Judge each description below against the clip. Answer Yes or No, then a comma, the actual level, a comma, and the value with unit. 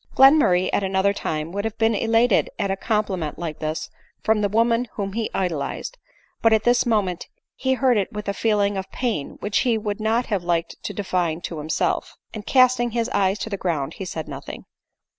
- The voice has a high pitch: Yes, high, 205 Hz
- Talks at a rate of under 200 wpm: No, fast, 205 wpm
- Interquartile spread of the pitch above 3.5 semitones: Yes, average, 4.0 semitones